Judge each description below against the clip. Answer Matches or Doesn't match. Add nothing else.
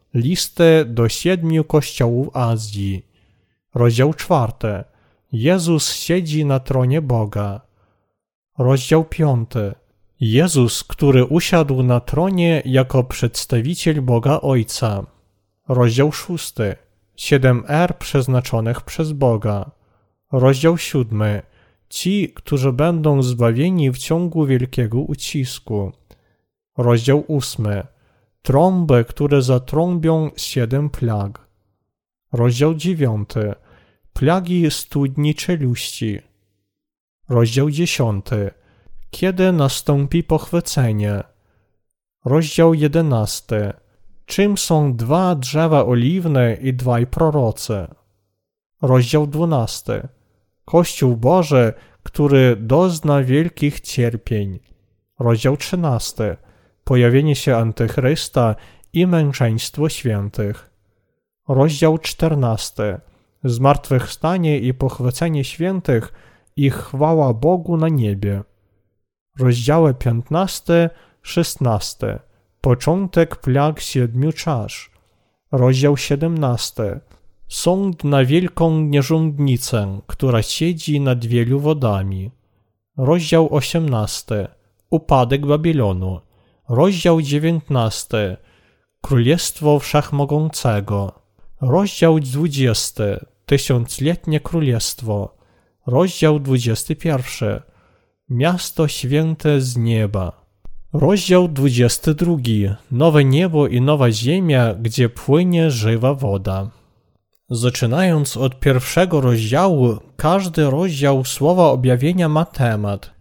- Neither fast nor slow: Doesn't match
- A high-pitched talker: Doesn't match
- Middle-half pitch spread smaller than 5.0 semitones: Doesn't match